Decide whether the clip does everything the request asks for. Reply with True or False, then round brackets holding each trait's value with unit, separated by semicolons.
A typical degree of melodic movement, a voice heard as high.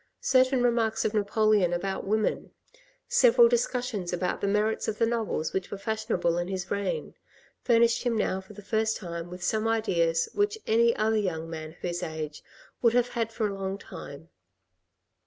True (4.3 semitones; 210 Hz)